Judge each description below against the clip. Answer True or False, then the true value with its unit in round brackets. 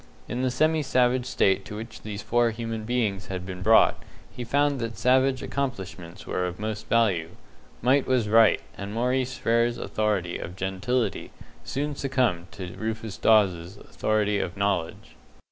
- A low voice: True (110 Hz)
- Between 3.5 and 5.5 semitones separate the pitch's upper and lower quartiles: True (4.3 semitones)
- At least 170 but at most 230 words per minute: False (155 wpm)